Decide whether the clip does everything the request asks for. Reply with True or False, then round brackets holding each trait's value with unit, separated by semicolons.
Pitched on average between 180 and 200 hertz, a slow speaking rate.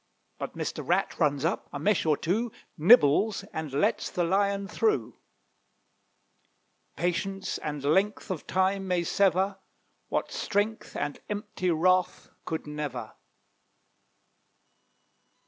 True (185 Hz; 110 wpm)